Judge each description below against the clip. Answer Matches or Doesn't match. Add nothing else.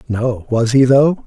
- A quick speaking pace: Doesn't match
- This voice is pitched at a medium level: Doesn't match